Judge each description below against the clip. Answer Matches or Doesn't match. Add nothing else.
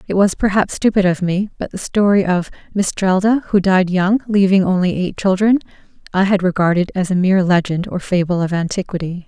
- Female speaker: Matches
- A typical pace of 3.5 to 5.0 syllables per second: Doesn't match